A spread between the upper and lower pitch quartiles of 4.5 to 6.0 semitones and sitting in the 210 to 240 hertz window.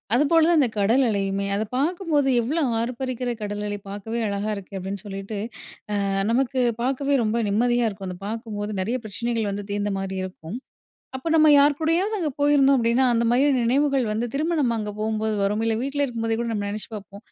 Yes: average, 4.9 semitones; high, 230 Hz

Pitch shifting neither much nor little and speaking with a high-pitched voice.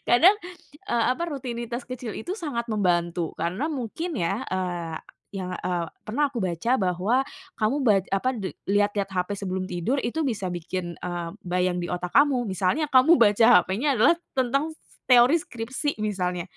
No: wide, 6.0 semitones; high, 215 Hz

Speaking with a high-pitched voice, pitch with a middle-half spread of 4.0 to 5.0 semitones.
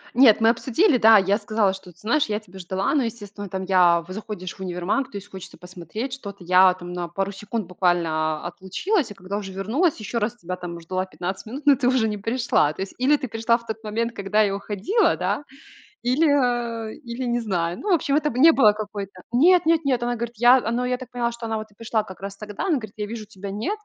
Yes: high, 215 Hz; average, 4.3 semitones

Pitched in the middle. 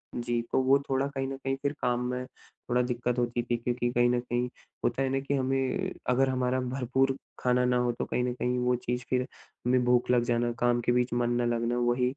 No: low, 125 Hz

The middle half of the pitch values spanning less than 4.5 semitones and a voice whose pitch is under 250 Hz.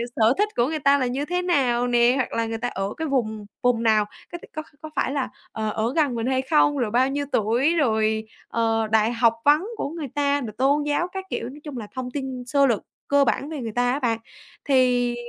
No: average, 3.9 semitones; very high, 255 Hz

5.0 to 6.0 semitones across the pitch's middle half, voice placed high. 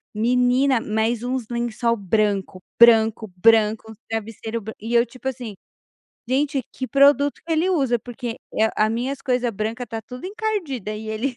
No: average, 2.9 semitones; high, 235 Hz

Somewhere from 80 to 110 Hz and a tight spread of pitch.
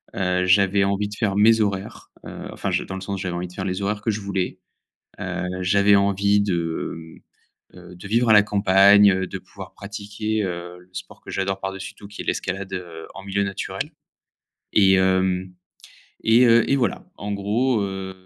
Yes: low, 100 Hz; narrow, 1.7 semitones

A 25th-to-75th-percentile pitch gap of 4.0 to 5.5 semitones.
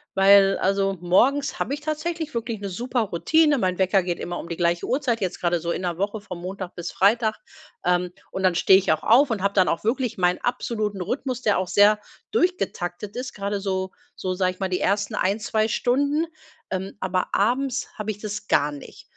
Yes: average, 4.6 semitones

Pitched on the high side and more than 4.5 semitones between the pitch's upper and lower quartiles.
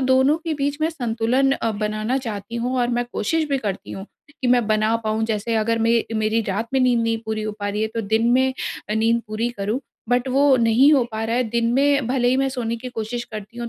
No: high, 230 Hz; average, 2.9 semitones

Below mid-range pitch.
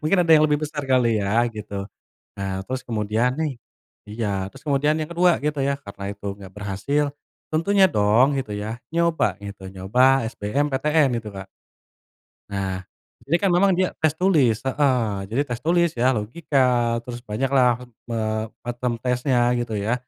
Yes: low, 125 Hz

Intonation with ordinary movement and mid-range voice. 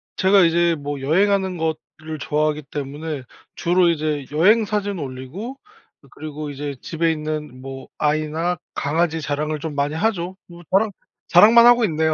Yes: average, 3.6 semitones; medium, 160 Hz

